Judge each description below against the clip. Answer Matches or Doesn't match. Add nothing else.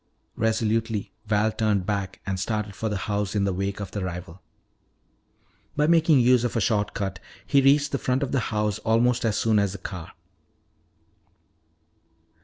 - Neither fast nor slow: Matches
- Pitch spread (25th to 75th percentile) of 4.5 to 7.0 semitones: Doesn't match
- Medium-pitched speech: Doesn't match